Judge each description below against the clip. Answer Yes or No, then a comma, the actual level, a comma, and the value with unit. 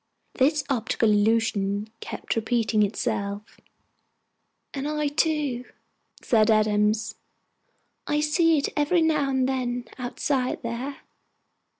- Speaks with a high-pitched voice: Yes, high, 245 Hz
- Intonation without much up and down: No, average, 4.9 semitones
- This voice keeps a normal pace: No, slow, 100 wpm